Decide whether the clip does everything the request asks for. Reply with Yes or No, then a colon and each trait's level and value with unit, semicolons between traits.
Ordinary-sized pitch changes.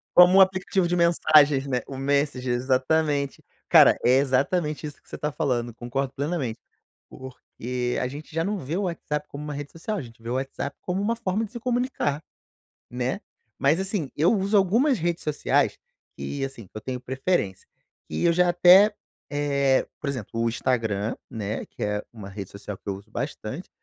No: wide, 5.8 semitones